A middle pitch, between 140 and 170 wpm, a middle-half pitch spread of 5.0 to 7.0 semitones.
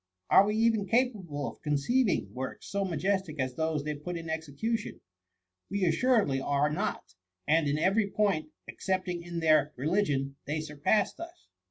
Yes: medium, 165 Hz; average, 160 wpm; wide, 5.4 semitones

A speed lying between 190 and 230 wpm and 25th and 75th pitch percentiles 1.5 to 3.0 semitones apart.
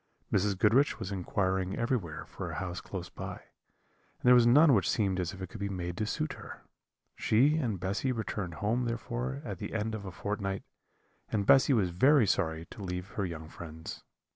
No: average, 195 wpm; average, 3.9 semitones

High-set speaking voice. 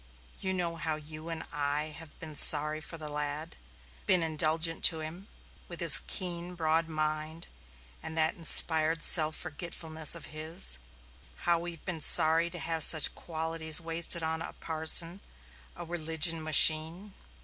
No: medium, 160 Hz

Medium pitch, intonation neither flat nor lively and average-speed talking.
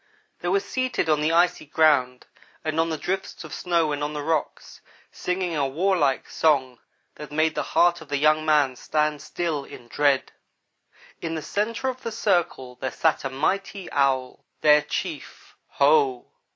Yes: medium, 155 Hz; average, 3.7 semitones; average, 170 wpm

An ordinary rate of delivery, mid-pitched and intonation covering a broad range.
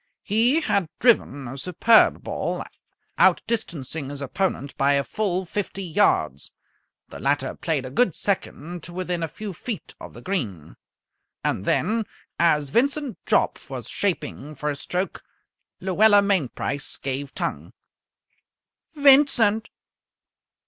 No: slow, 125 wpm; medium, 180 Hz; wide, 7.1 semitones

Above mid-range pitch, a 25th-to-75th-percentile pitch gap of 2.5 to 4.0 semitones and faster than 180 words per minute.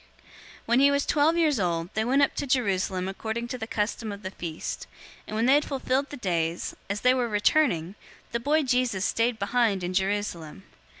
No: high, 225 Hz; wide, 5.4 semitones; fast, 205 wpm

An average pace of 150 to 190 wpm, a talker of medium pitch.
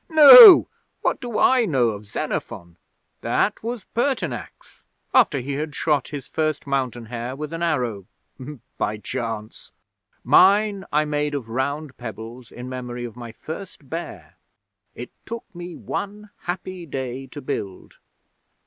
No: average, 140 wpm; medium, 145 Hz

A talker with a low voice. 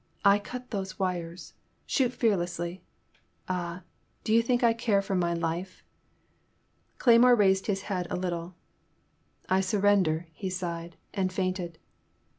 No: medium, 185 Hz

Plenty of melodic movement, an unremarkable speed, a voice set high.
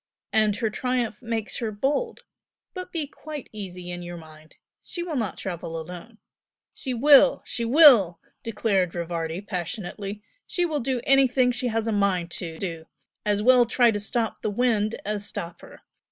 Yes: wide, 5.7 semitones; average, 170 wpm; high, 215 Hz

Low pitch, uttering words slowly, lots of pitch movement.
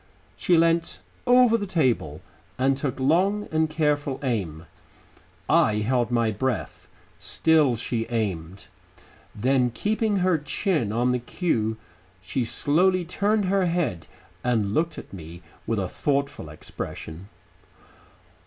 Yes: low, 130 Hz; slow, 125 wpm; wide, 7.5 semitones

